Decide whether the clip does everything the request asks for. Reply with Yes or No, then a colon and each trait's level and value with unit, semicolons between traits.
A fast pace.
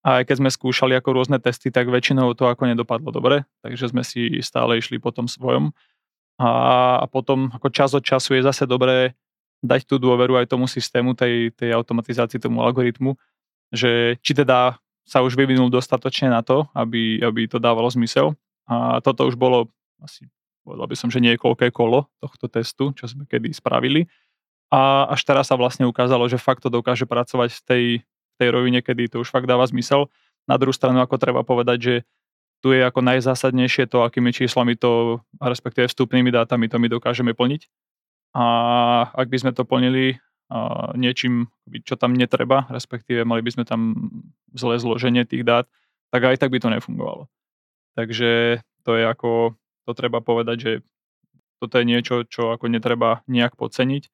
Yes: fast, 175 wpm